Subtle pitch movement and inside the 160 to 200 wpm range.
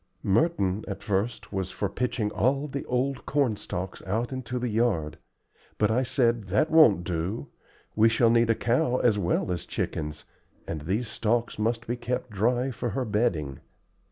No: average, 4.1 semitones; average, 170 wpm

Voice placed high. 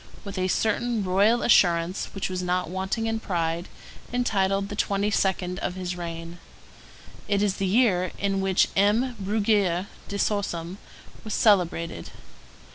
Yes: high, 195 Hz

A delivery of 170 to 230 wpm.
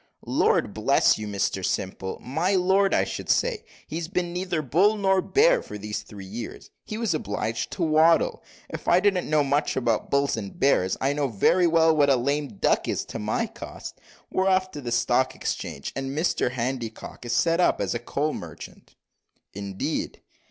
Yes: average, 180 wpm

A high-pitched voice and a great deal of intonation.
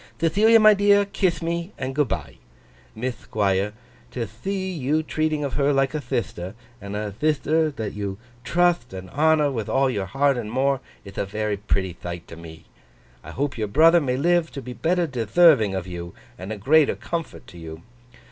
No: low, 130 Hz; wide, 7.7 semitones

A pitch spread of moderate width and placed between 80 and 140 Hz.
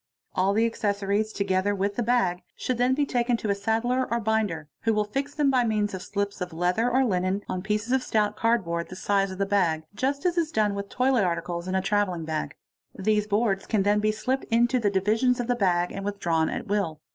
No: average, 3.8 semitones; high, 205 Hz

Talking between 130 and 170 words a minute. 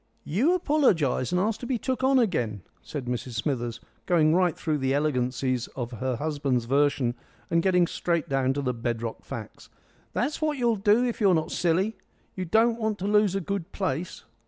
No: average, 185 wpm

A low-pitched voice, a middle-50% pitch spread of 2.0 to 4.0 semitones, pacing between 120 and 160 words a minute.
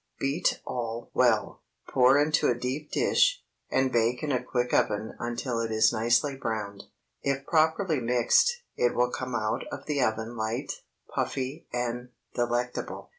Yes: low, 125 Hz; average, 2.9 semitones; average, 150 wpm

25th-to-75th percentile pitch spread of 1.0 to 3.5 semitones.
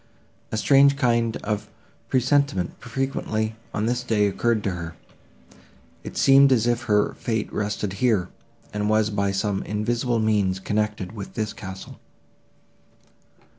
Yes: average, 2.9 semitones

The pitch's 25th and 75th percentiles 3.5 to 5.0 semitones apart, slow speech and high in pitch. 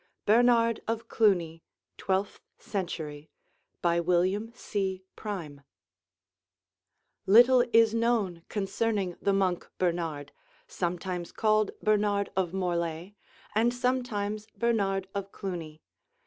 Yes: average, 3.9 semitones; slow, 95 wpm; high, 195 Hz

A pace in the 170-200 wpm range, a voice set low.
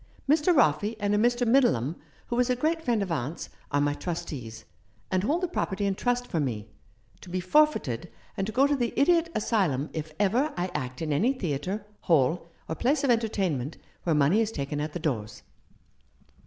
No: average, 195 wpm; high, 190 Hz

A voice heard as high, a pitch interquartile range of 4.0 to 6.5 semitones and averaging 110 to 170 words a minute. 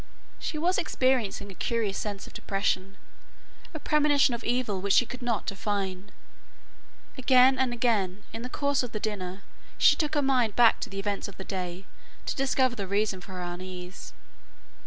No: high, 215 Hz; average, 4.7 semitones; average, 180 wpm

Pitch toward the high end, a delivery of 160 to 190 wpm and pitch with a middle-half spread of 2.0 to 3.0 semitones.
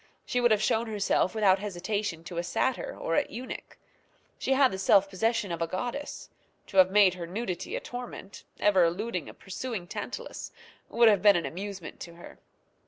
No: high, 200 Hz; average, 185 wpm; average, 3.8 semitones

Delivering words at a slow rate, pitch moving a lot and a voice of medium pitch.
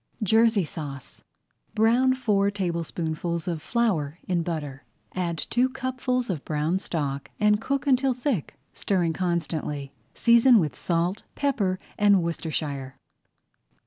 Yes: slow, 125 wpm; wide, 6.5 semitones; medium, 180 Hz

